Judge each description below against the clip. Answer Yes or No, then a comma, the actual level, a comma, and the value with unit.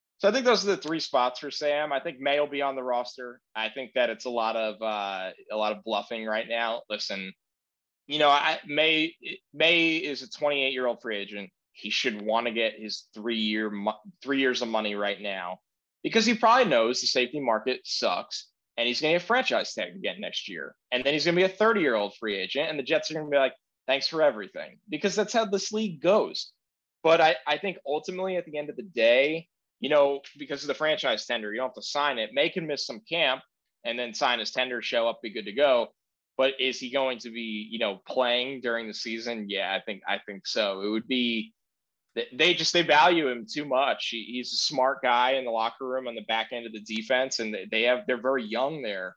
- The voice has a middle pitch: No, low, 125 Hz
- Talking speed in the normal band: No, fast, 235 wpm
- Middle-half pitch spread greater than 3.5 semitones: Yes, average, 5.2 semitones